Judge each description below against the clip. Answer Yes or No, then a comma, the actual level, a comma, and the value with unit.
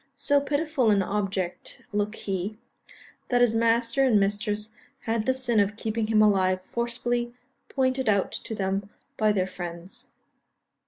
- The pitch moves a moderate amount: Yes, average, 3.3 semitones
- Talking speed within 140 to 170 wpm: Yes, average, 145 wpm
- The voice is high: Yes, high, 215 Hz